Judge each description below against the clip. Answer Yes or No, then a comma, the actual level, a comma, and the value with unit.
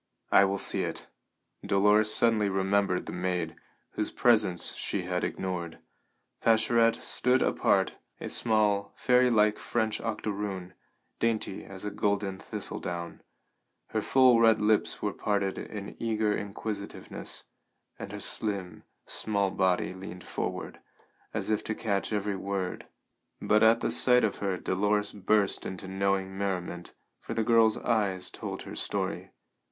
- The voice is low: Yes, low, 100 Hz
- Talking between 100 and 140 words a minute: Yes, slow, 135 wpm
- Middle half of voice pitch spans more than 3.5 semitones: No, narrow, 2.4 semitones